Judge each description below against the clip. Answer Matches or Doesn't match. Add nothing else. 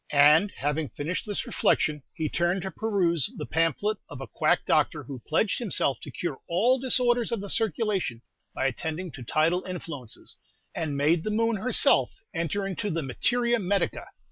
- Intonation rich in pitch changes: Matches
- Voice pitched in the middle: Matches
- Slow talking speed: Doesn't match